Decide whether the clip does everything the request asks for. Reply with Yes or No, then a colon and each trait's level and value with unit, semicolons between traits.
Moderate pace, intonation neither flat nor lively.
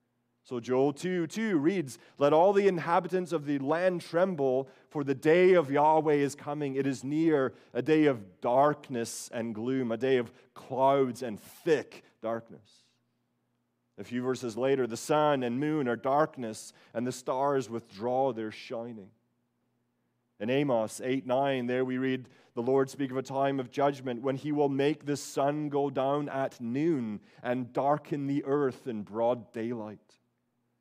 Yes: average, 160 wpm; average, 3.5 semitones